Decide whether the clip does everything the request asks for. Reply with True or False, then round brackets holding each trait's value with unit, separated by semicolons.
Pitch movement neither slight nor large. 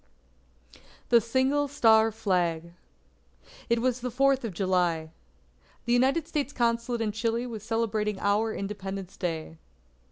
True (3.9 semitones)